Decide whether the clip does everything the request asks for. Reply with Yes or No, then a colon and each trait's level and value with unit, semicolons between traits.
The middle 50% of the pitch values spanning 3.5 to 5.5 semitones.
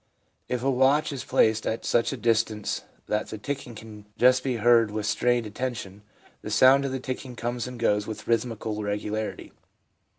No: average, 2.9 semitones